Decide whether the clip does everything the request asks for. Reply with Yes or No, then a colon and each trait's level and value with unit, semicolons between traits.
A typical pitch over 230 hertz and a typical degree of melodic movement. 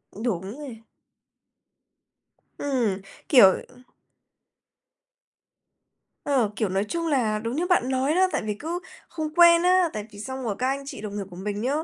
No: very high, 250 Hz; wide, 6.4 semitones